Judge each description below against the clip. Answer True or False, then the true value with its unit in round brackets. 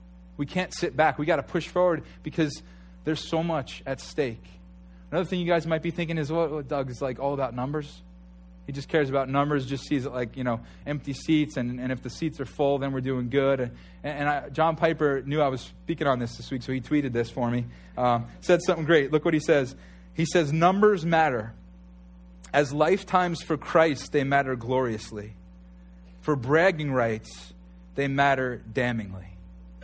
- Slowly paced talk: False (200 wpm)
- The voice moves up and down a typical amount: False (6.0 semitones)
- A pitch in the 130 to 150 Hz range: True (140 Hz)